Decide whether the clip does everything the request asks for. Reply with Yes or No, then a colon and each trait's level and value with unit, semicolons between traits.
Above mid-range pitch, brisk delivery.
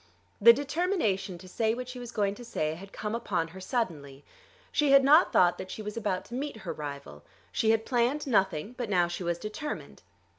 Yes: high, 210 Hz; fast, 210 wpm